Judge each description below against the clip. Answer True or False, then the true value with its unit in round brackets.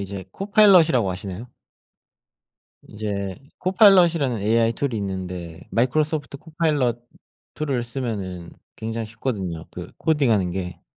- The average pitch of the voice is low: True (115 Hz)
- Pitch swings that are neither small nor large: False (7.5 semitones)